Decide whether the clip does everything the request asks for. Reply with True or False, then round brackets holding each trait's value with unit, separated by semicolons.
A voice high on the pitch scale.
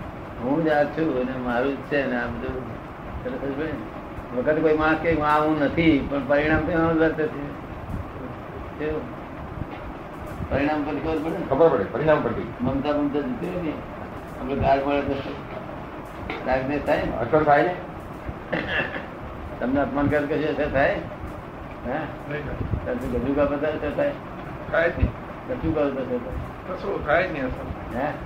False (145 Hz)